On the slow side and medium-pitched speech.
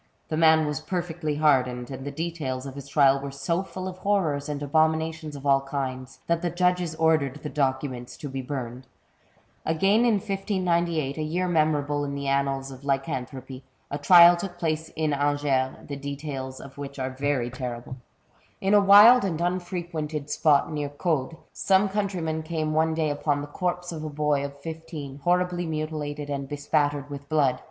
No: average, 175 wpm; medium, 150 Hz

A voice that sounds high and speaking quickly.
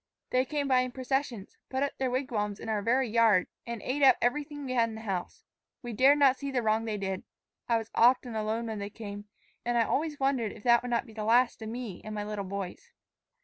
Yes: high, 235 Hz; fast, 240 wpm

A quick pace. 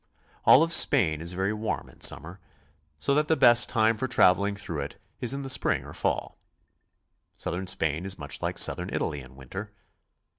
No: average, 190 wpm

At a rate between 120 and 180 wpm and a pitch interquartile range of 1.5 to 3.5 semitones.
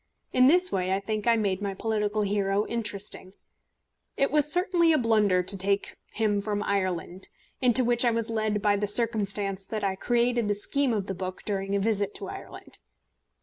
No: average, 190 wpm; average, 2.9 semitones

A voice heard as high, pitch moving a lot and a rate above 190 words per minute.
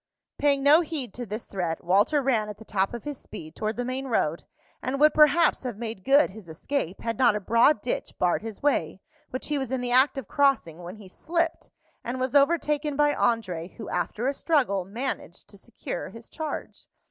Yes: high, 245 Hz; wide, 5.7 semitones; fast, 205 wpm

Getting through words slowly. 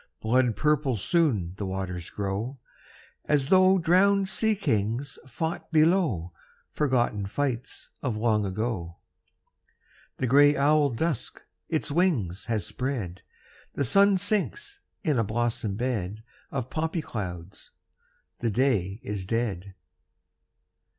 Yes: slow, 115 wpm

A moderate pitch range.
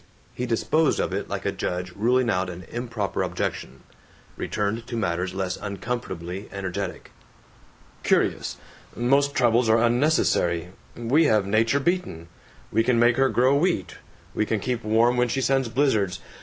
Yes: average, 4.4 semitones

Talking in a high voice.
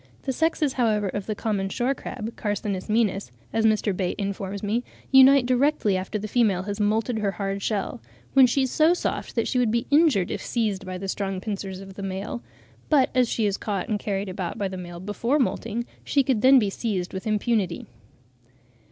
Yes: high, 210 Hz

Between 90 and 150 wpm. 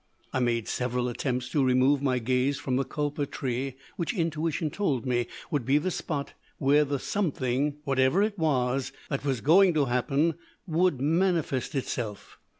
No: average, 160 wpm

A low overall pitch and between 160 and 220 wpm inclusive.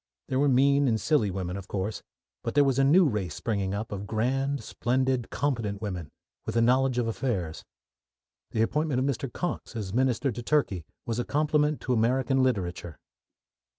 Yes: low, 120 Hz; average, 180 wpm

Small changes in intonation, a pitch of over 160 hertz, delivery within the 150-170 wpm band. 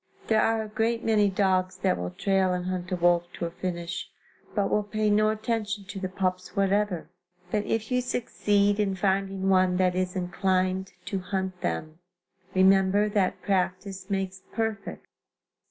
Yes: narrow, 2.1 semitones; high, 190 Hz; average, 165 wpm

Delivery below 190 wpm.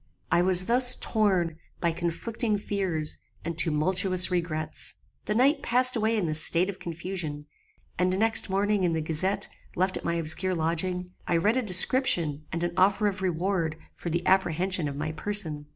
Yes: average, 170 wpm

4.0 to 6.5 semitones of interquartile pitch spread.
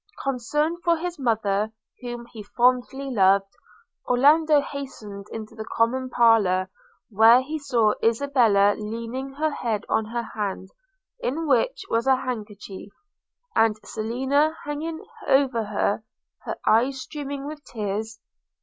Yes: average, 4.4 semitones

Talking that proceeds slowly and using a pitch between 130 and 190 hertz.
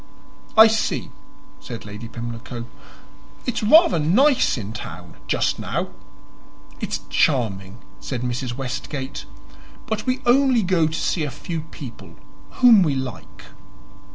Yes: slow, 125 wpm; medium, 140 Hz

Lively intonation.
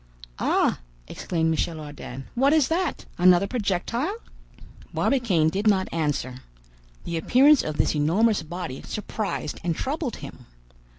Yes: wide, 7.7 semitones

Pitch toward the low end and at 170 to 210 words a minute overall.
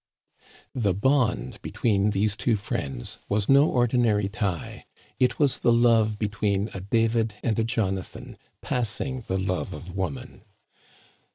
No: low, 110 Hz; average, 150 wpm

